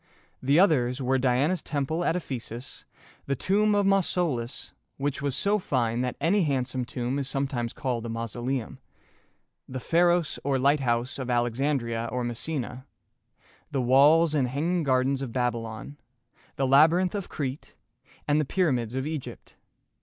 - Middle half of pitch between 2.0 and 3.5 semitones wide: No, average, 3.9 semitones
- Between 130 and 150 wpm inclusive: Yes, average, 145 wpm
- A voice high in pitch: No, low, 135 Hz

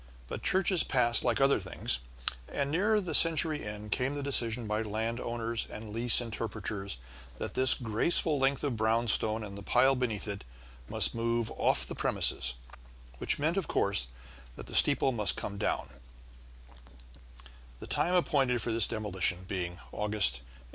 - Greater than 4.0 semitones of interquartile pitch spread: Yes, average, 4.5 semitones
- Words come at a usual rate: Yes, average, 155 wpm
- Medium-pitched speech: No, low, 115 Hz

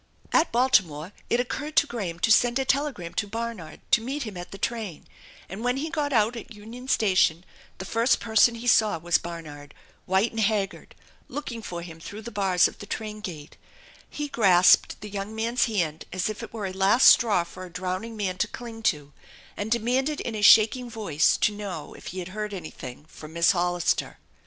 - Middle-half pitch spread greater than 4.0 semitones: Yes, average, 4.7 semitones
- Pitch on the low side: No, high, 210 Hz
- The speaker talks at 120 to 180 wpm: No, average, 200 wpm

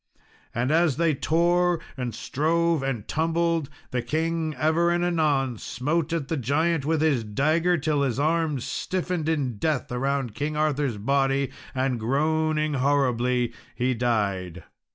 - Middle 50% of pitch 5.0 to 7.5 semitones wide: No, average, 4.2 semitones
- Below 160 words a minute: Yes, average, 140 wpm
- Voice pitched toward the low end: No, medium, 145 Hz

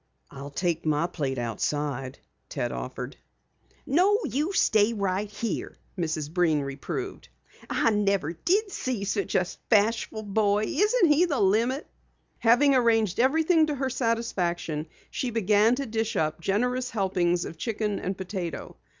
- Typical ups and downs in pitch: No, wide, 6.3 semitones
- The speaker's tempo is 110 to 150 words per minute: Yes, average, 140 wpm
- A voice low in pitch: No, high, 210 Hz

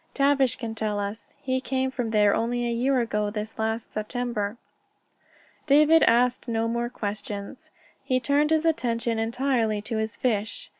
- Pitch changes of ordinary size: Yes, average, 3.0 semitones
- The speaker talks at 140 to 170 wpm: Yes, average, 155 wpm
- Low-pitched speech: No, high, 235 Hz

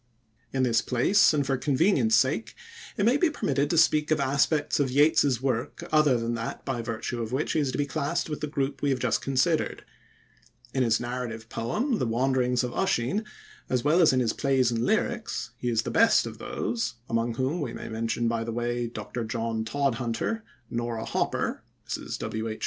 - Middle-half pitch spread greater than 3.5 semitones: Yes, average, 3.9 semitones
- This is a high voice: No, low, 130 Hz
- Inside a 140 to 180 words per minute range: No, average, 200 wpm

